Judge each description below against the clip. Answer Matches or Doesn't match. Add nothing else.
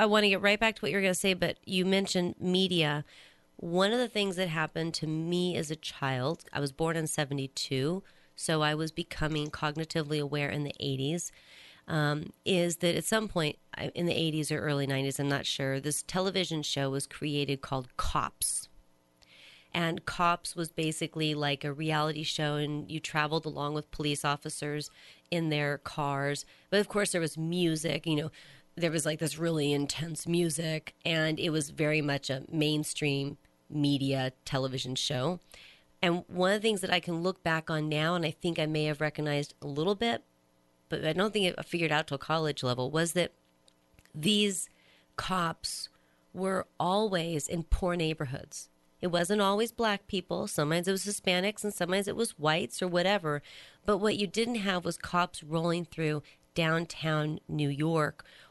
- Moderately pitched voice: Matches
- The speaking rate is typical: Matches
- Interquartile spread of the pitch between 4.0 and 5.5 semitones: Doesn't match